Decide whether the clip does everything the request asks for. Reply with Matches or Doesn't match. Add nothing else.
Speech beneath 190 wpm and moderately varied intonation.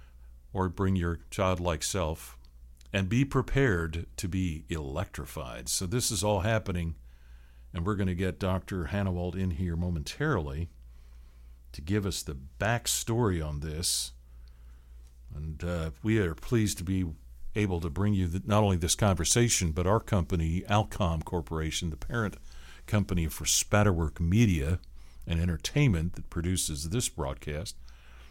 Doesn't match